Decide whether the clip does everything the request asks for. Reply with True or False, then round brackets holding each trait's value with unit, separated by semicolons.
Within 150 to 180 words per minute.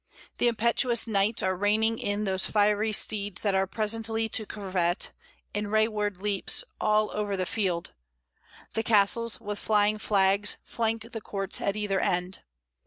True (165 wpm)